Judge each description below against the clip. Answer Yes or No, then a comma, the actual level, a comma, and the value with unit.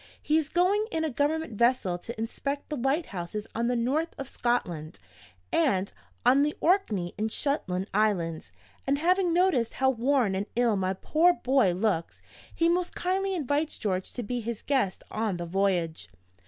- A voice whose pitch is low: No, high, 245 Hz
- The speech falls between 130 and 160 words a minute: No, average, 170 wpm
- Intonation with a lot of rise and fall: Yes, wide, 7.7 semitones